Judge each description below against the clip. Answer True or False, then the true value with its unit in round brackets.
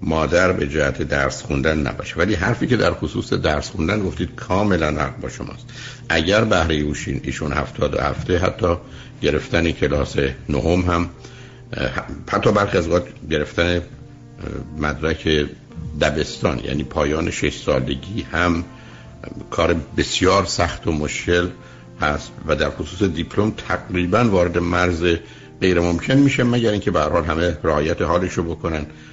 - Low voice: True (85 Hz)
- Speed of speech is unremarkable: True (135 wpm)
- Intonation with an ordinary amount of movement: True (3.9 semitones)